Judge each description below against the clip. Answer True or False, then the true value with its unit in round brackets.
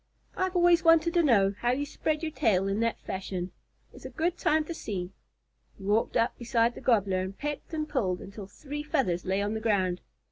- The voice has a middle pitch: False (230 Hz)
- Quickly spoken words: True (210 wpm)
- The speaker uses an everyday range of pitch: False (7.8 semitones)